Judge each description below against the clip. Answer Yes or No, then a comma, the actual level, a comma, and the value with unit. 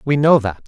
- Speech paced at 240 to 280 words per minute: Yes, fast, 270 wpm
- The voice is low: Yes, low, 130 Hz